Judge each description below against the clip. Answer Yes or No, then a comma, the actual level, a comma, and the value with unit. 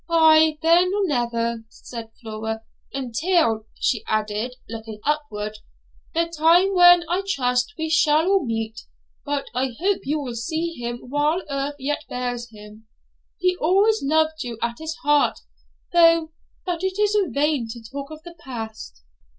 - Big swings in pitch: Yes, wide, 6.1 semitones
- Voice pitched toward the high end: Yes, very high, 285 Hz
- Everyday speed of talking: Yes, average, 150 wpm